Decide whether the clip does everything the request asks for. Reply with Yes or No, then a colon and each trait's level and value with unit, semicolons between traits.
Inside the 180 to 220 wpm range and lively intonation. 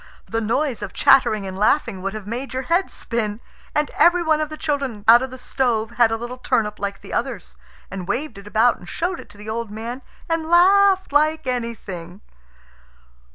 Yes: average, 200 wpm; wide, 6.1 semitones